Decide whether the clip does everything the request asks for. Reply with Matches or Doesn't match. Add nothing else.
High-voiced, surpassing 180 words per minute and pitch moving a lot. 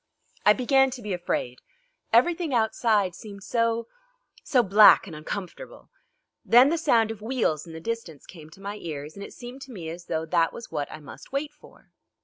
Matches